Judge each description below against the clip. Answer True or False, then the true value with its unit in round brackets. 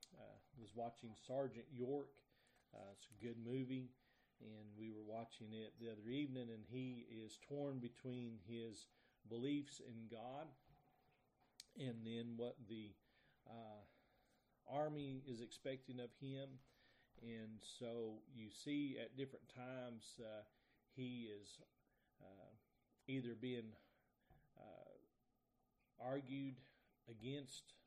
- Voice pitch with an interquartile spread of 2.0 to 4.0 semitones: True (2.6 semitones)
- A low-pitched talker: True (120 Hz)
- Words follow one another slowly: True (115 wpm)